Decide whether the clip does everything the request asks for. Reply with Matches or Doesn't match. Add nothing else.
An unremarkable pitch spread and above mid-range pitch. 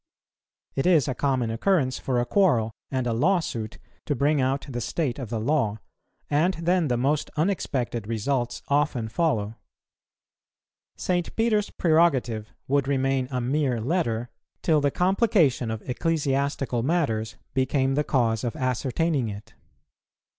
Doesn't match